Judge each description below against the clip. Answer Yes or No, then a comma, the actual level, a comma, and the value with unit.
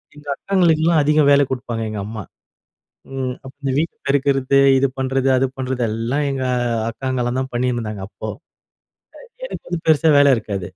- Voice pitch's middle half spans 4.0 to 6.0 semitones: No, average, 2.9 semitones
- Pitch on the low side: Yes, low, 130 Hz